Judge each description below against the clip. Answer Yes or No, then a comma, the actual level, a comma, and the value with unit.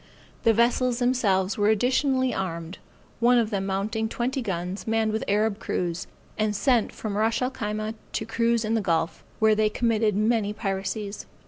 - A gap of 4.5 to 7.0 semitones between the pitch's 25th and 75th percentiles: No, average, 2.7 semitones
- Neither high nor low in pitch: No, high, 215 Hz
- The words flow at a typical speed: Yes, average, 165 wpm